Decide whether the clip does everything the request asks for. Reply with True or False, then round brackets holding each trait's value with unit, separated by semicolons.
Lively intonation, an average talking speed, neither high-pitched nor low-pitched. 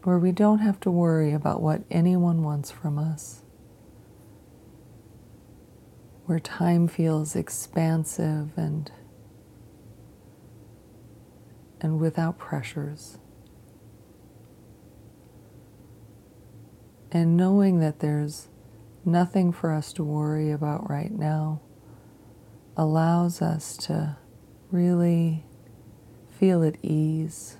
False (6.4 semitones; 85 wpm; 155 Hz)